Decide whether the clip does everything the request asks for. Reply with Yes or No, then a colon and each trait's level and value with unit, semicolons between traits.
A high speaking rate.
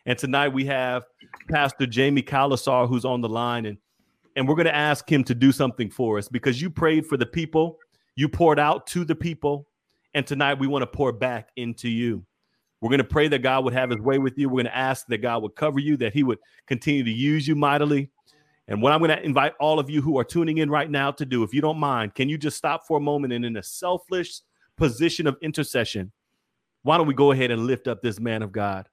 Yes: fast, 250 wpm